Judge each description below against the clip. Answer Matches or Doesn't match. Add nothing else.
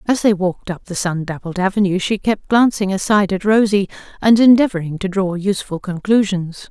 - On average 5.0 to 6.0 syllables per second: Matches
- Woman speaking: Matches